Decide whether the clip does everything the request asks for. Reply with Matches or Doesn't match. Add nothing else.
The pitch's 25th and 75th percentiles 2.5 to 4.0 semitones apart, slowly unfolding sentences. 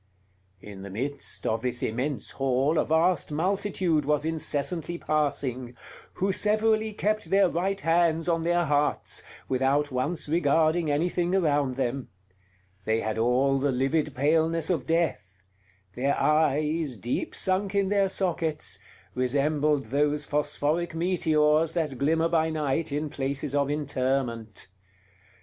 Matches